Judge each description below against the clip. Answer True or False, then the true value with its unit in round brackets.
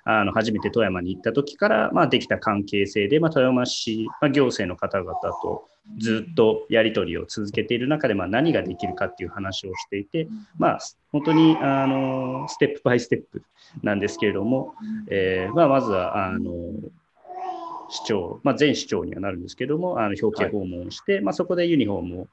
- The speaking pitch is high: False (125 Hz)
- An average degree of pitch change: False (7.1 semitones)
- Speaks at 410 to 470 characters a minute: False (365 characters per minute)